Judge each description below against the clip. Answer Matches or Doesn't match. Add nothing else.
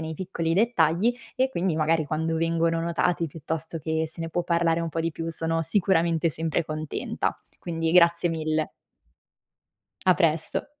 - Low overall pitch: Doesn't match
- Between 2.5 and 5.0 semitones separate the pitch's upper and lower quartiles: Doesn't match